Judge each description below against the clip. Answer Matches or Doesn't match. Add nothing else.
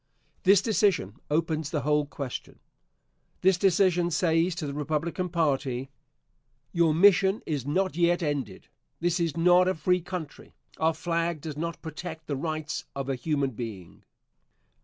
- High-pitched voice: Doesn't match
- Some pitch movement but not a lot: Matches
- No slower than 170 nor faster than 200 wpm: Doesn't match